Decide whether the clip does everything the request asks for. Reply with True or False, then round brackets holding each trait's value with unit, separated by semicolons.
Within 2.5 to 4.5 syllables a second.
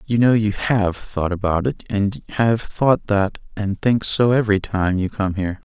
True (4.4 syllables/s)